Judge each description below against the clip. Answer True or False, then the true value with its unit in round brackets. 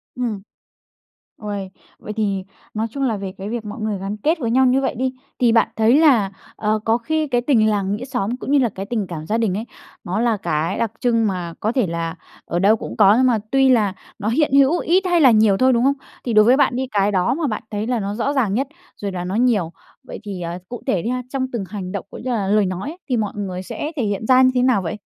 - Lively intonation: False (4.3 semitones)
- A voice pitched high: True (220 Hz)